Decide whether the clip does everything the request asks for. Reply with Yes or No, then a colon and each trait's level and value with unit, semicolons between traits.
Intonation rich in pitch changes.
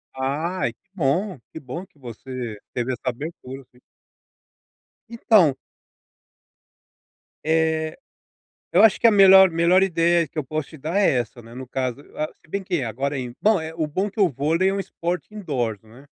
Yes: wide, 6.0 semitones